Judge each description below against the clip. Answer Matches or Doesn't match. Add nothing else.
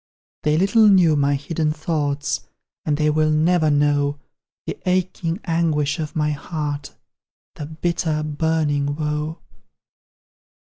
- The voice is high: Doesn't match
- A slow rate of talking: Matches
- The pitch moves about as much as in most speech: Doesn't match